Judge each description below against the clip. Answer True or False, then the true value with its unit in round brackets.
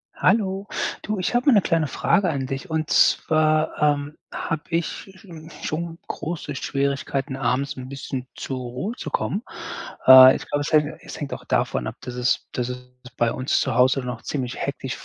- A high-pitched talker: False (145 Hz)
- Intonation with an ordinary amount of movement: True (4.1 semitones)